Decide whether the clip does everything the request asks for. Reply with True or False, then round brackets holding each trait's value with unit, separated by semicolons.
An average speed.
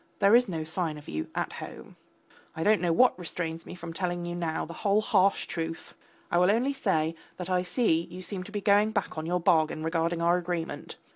False (220 wpm)